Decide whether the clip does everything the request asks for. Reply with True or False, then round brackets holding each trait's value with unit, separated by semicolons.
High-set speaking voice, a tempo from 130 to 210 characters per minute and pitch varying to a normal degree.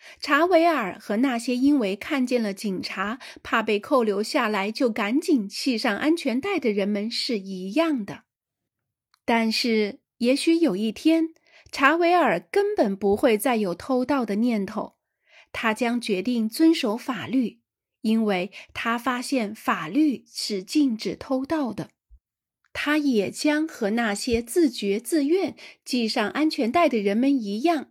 False (245 Hz; 205 characters per minute; 6.0 semitones)